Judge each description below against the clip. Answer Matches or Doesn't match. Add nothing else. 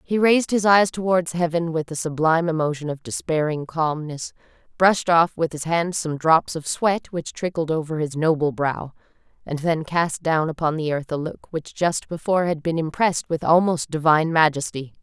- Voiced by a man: Doesn't match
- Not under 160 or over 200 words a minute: Matches